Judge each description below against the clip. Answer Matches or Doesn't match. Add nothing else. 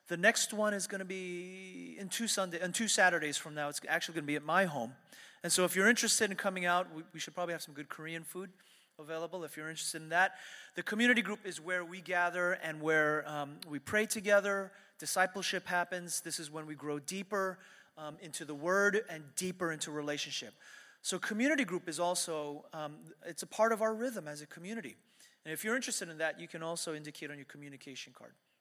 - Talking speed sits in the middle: Doesn't match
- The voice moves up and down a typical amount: Matches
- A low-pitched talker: Doesn't match